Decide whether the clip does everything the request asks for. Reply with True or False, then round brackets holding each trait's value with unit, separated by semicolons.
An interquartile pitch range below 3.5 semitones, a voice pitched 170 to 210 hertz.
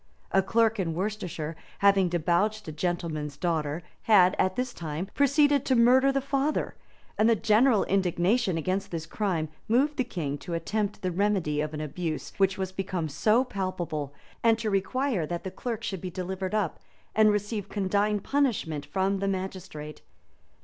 False (4.2 semitones; 190 Hz)